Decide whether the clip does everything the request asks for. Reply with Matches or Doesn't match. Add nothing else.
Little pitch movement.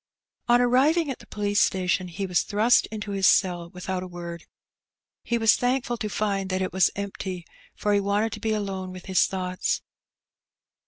Doesn't match